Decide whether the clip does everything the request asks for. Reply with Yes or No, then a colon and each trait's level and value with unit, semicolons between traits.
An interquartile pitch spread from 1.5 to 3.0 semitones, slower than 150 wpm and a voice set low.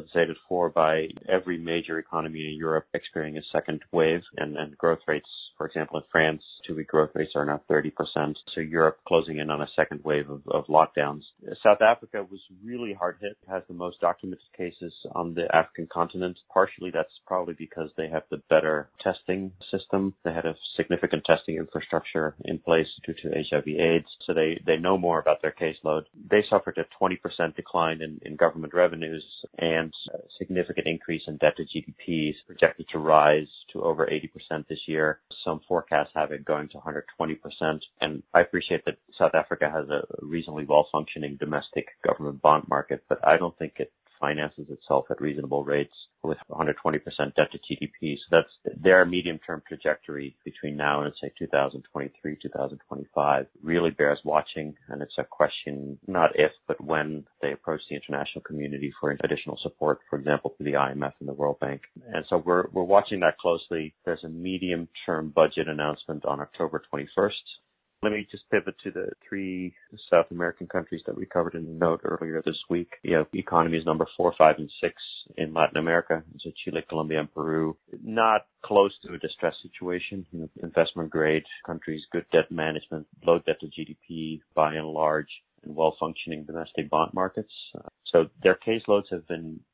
No: narrow, 2.4 semitones; average, 175 wpm; very low, 80 Hz